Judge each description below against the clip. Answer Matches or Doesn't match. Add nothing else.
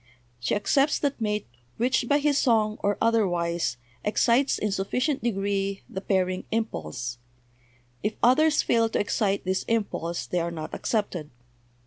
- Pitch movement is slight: Doesn't match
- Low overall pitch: Doesn't match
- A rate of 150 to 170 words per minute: Doesn't match